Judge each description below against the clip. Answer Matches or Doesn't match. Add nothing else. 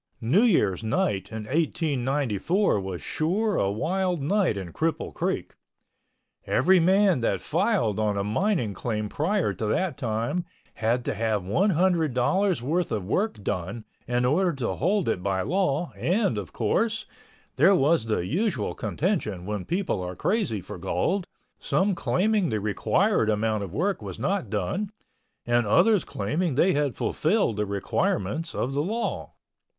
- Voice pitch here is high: Doesn't match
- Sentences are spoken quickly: Doesn't match